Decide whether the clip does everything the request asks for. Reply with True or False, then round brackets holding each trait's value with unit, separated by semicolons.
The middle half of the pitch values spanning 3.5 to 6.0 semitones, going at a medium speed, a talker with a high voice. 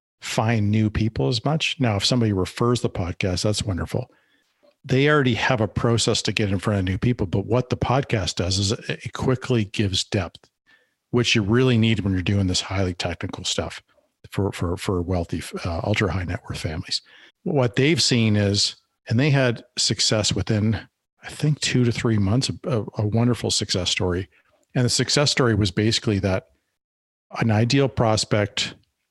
False (3.9 semitones; 175 wpm; 110 Hz)